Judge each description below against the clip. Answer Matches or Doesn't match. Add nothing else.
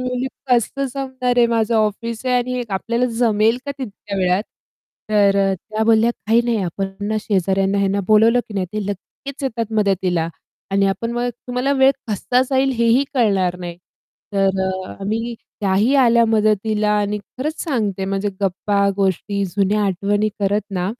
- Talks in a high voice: Matches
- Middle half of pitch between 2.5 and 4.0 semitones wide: Matches